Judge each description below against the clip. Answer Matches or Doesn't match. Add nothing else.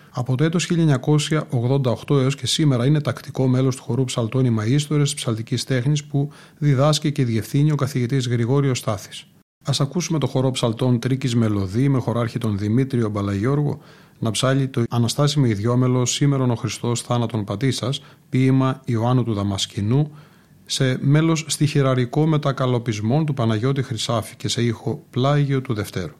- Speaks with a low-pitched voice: Matches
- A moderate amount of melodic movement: Matches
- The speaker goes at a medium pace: Matches